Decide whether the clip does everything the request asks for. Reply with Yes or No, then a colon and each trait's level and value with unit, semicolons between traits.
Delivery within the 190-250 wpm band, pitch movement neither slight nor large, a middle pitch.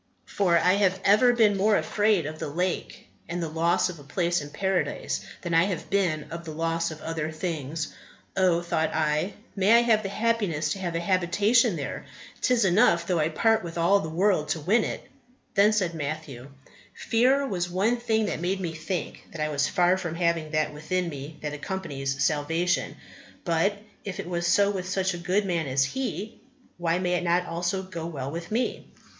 Yes: average, 200 wpm; average, 3.6 semitones; medium, 175 Hz